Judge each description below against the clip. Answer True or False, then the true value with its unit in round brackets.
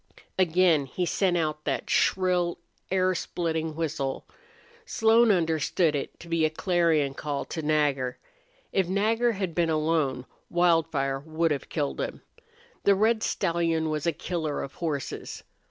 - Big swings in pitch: False (2.9 semitones)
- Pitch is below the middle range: False (165 Hz)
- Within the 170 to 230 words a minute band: False (140 wpm)